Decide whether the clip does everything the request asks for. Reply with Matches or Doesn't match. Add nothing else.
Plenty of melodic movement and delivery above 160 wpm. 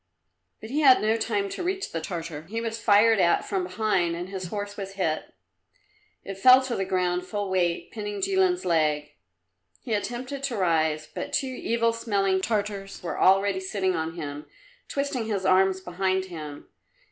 Doesn't match